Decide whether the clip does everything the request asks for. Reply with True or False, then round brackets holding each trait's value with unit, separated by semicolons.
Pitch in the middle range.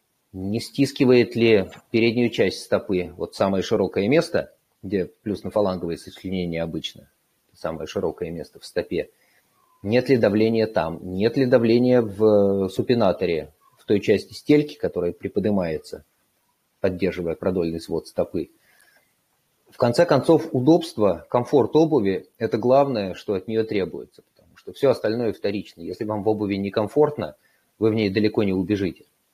False (110 Hz)